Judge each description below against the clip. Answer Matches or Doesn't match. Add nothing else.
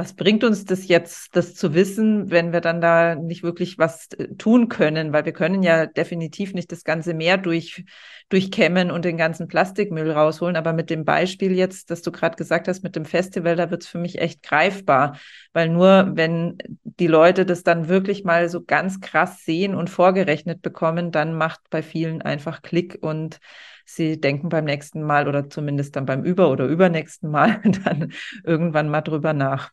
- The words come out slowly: Doesn't match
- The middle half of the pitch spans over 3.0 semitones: Doesn't match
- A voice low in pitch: Doesn't match